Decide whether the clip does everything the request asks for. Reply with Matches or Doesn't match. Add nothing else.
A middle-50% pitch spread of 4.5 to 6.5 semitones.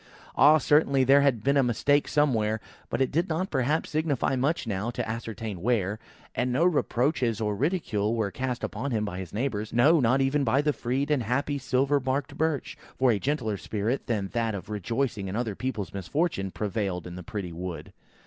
Matches